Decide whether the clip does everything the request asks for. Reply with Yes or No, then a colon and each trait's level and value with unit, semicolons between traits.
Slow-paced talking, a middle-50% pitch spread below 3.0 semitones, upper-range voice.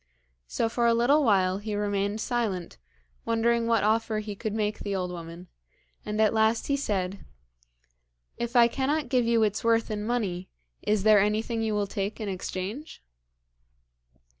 No: average, 165 wpm; narrow, 2.5 semitones; high, 215 Hz